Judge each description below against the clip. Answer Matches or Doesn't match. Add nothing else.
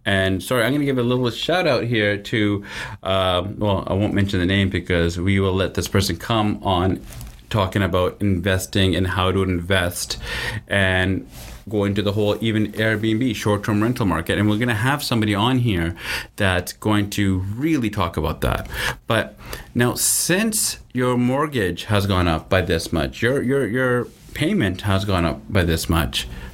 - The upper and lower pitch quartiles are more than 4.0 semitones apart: Doesn't match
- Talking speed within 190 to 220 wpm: Doesn't match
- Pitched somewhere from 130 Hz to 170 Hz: Doesn't match